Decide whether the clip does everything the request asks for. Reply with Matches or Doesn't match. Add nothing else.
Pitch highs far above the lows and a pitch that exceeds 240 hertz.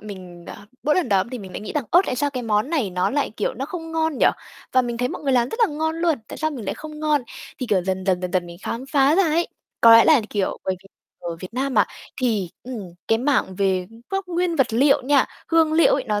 Matches